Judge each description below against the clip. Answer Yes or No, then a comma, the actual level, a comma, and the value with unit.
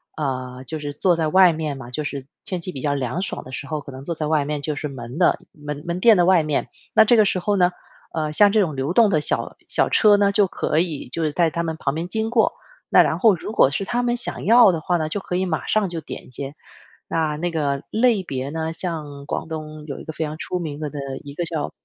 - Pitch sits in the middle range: Yes, medium, 160 Hz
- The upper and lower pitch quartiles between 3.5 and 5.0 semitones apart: Yes, average, 4.0 semitones